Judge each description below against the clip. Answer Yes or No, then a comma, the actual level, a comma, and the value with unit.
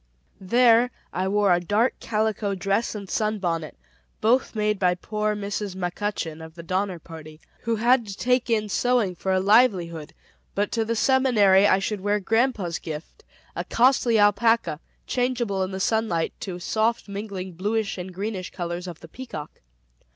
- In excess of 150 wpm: Yes, average, 165 wpm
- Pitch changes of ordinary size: Yes, average, 3.5 semitones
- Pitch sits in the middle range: No, high, 205 Hz